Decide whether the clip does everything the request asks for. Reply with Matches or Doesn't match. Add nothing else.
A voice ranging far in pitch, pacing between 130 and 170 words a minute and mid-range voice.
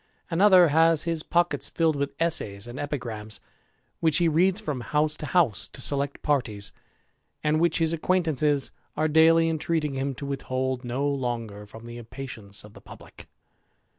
Doesn't match